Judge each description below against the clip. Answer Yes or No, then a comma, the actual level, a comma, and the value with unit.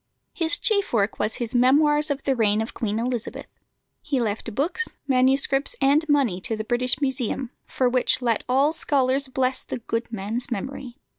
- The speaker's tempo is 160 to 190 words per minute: Yes, average, 170 wpm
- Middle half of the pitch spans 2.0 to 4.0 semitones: Yes, average, 3.3 semitones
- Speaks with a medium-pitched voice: No, very high, 255 Hz